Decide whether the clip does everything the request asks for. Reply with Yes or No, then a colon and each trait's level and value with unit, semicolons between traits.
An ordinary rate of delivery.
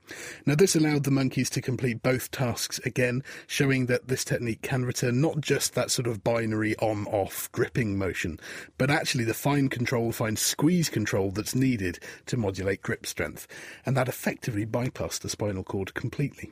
Yes: average, 175 wpm